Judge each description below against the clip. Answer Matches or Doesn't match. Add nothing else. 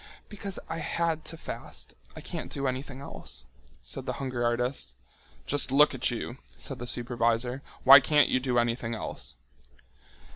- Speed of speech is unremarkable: Matches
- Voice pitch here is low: Matches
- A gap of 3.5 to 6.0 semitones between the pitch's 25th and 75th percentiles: Doesn't match